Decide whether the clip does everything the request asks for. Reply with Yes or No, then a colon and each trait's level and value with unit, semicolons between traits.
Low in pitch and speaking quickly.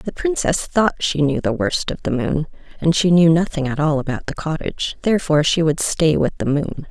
No: medium, 160 Hz; fast, 225 wpm